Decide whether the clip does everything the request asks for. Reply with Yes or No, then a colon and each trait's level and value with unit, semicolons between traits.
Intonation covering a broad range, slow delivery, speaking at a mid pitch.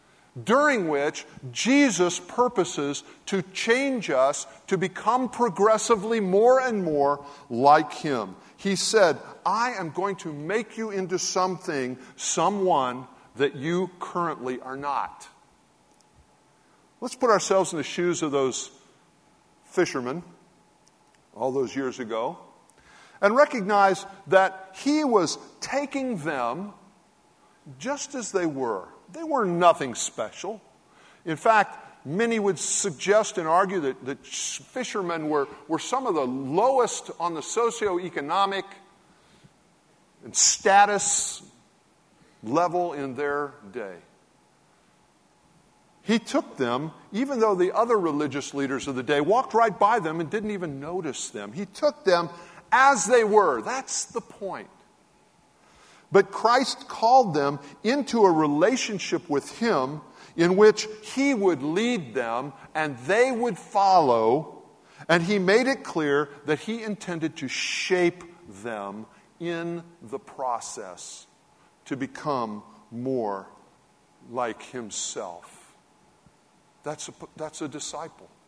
Yes: wide, 6.8 semitones; slow, 120 wpm; medium, 180 Hz